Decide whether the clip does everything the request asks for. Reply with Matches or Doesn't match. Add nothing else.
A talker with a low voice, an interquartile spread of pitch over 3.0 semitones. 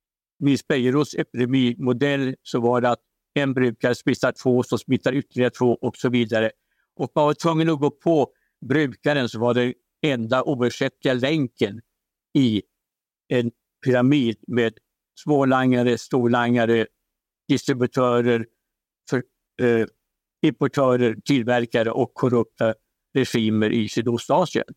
Doesn't match